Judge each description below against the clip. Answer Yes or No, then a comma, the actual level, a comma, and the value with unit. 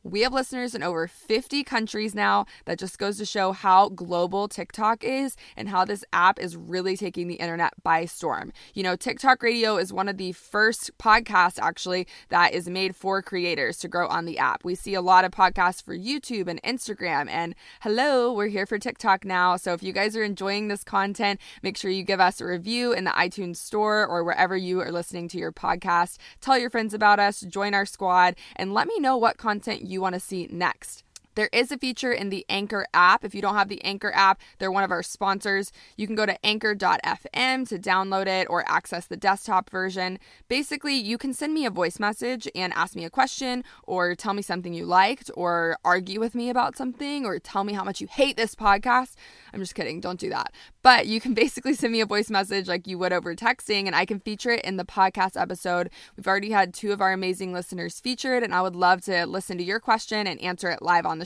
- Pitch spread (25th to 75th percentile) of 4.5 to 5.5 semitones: No, average, 3.4 semitones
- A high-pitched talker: Yes, high, 195 Hz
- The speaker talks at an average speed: No, fast, 230 wpm